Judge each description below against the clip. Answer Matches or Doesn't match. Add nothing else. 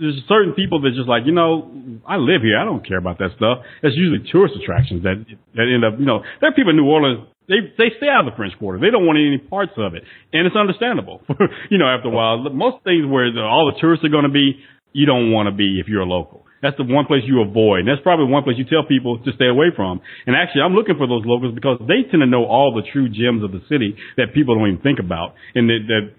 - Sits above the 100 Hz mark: Matches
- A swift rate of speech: Matches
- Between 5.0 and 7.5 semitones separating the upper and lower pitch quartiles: Matches